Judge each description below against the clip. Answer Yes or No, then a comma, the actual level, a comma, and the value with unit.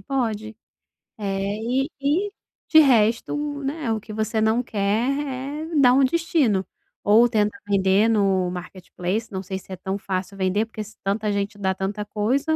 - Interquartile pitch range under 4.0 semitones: No, average, 4.6 semitones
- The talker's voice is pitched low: No, high, 215 Hz